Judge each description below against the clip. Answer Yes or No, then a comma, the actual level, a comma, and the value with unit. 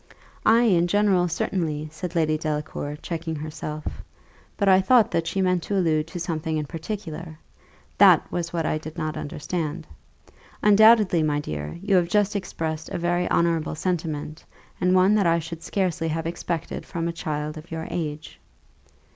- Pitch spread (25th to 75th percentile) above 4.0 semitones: No, average, 2.7 semitones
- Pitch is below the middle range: No, medium, 165 Hz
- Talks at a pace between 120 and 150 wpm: No, average, 165 wpm